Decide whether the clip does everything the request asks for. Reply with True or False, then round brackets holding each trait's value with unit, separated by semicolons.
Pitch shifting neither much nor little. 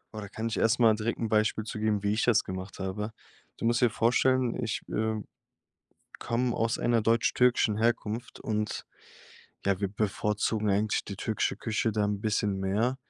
False (1.9 semitones)